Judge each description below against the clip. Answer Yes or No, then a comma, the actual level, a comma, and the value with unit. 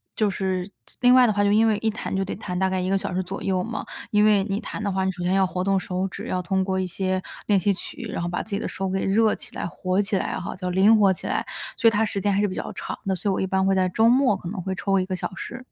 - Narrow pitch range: Yes, narrow, 1.9 semitones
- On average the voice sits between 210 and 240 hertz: No, high, 195 Hz